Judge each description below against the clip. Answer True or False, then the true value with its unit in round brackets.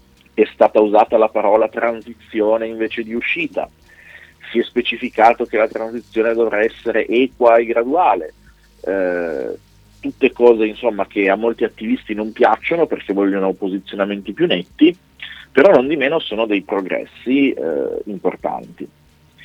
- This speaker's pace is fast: False (135 wpm)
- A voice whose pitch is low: True (115 Hz)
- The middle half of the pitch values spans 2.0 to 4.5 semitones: True (2.8 semitones)